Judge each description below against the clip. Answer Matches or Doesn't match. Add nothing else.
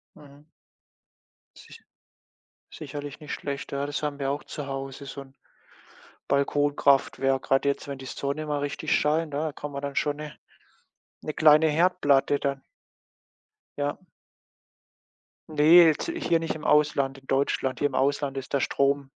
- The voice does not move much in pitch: Matches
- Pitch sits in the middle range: Matches